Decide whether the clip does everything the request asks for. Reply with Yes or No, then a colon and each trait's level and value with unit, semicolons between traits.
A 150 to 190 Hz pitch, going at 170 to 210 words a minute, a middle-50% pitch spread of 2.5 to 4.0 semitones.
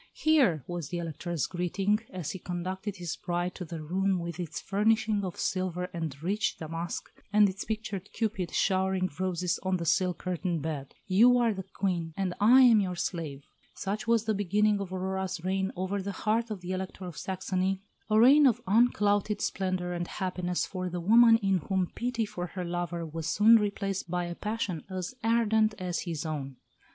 Yes: medium, 185 Hz; average, 185 wpm; average, 3.0 semitones